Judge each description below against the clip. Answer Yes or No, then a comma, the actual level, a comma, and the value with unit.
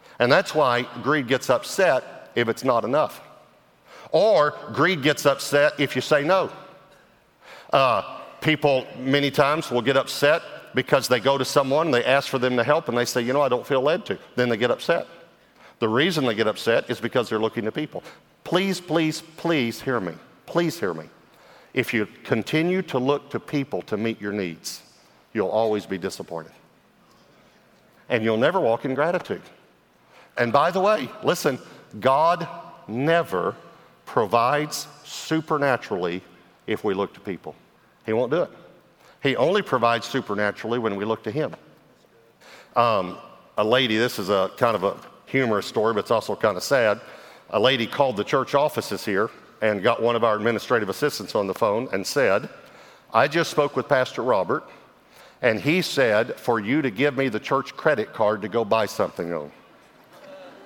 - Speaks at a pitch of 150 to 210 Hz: No, low, 130 Hz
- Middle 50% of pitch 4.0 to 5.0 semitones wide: Yes, average, 4.7 semitones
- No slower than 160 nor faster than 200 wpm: Yes, average, 175 wpm